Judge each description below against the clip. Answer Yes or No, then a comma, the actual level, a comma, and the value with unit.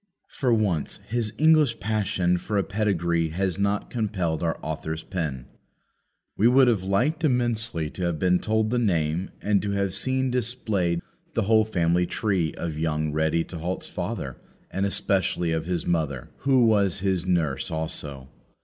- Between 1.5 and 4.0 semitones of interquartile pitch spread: No, average, 4.9 semitones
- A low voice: Yes, very low, 95 Hz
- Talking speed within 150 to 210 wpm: Yes, average, 160 wpm